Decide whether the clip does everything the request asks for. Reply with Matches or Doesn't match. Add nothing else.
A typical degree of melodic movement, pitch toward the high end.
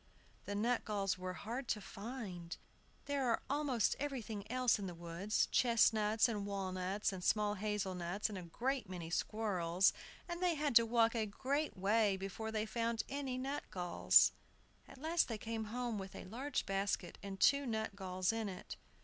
Matches